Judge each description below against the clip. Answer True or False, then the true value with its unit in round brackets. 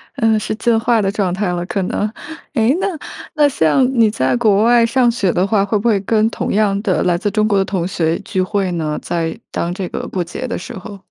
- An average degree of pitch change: True (3.7 semitones)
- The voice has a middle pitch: False (205 Hz)